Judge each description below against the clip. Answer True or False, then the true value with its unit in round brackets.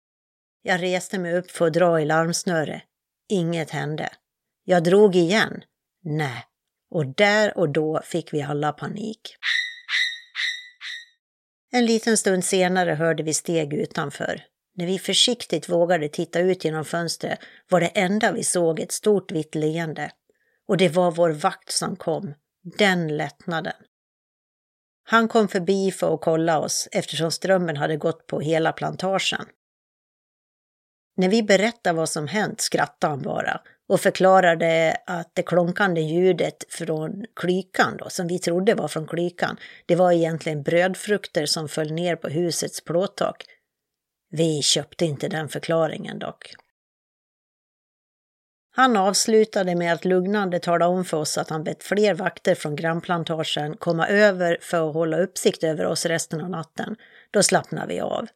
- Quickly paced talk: False (145 wpm)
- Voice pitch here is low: False (175 Hz)